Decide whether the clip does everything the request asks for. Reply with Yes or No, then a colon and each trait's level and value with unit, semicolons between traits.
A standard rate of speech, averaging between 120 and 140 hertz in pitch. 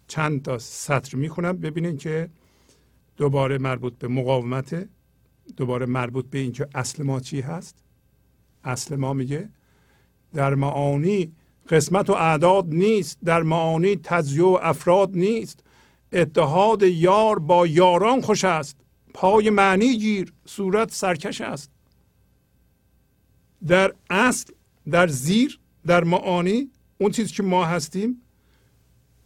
No: average, 115 wpm; medium, 170 Hz